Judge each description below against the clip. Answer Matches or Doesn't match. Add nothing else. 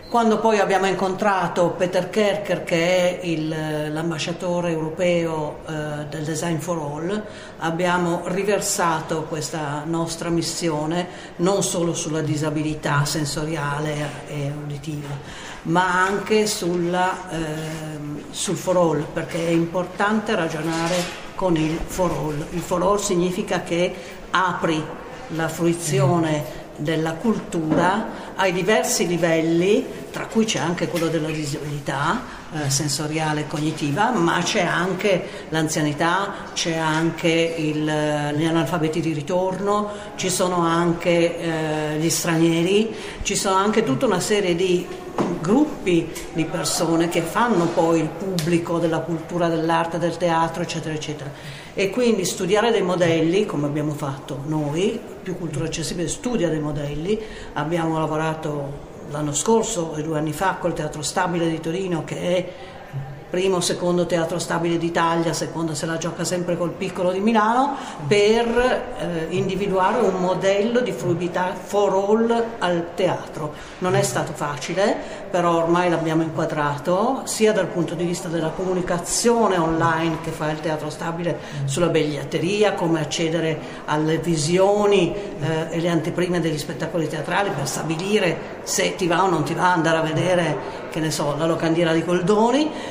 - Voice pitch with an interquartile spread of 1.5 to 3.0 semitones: Matches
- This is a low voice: Doesn't match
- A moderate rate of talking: Matches